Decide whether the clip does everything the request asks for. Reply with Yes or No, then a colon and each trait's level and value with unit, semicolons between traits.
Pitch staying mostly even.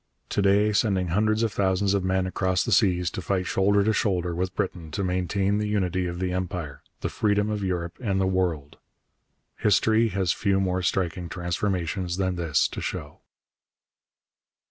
Yes: narrow, 2.2 semitones